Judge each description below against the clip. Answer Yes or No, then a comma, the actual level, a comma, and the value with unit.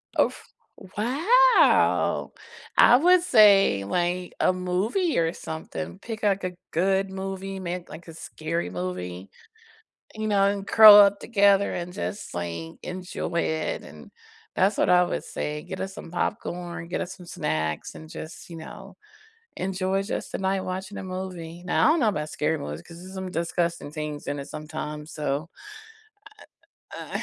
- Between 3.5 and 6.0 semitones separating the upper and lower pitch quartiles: Yes, average, 3.8 semitones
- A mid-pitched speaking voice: Yes, medium, 180 Hz